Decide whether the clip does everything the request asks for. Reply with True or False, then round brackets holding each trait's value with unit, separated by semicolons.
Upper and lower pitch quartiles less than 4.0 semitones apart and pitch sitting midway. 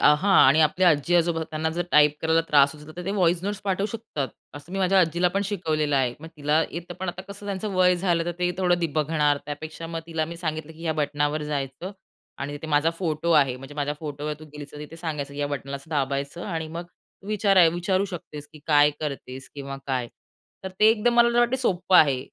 True (3.4 semitones; 160 Hz)